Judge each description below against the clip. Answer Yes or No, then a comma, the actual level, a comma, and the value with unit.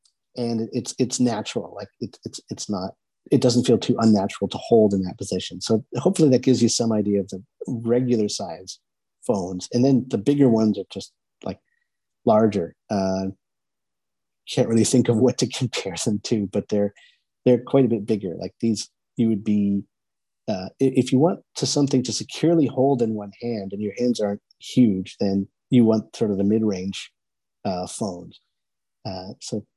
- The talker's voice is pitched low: Yes, low, 115 Hz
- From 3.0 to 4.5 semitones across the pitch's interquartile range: Yes, average, 3.8 semitones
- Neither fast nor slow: Yes, average, 180 wpm